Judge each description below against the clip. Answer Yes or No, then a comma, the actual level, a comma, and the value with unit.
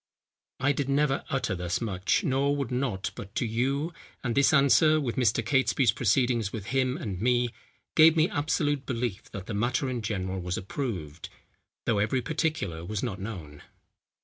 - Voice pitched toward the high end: No, low, 120 Hz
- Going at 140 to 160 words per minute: No, average, 170 wpm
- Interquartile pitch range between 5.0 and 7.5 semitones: Yes, wide, 5.4 semitones